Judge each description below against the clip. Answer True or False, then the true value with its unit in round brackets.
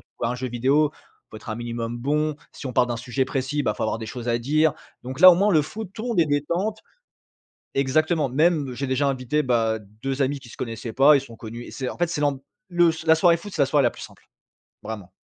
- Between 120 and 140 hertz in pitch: True (135 Hz)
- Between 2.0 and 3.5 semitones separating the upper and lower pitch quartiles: False (4.4 semitones)